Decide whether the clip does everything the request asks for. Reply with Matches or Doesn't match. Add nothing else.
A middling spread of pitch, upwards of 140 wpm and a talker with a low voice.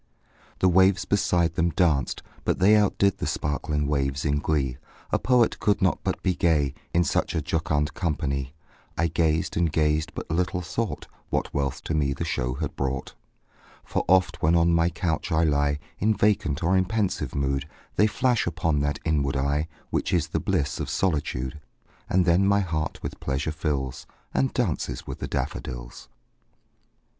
Matches